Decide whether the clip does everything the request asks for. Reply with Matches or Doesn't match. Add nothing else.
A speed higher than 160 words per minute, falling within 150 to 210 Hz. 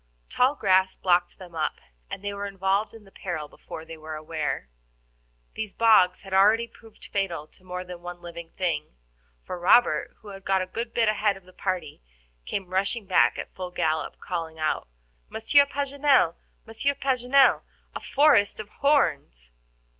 Matches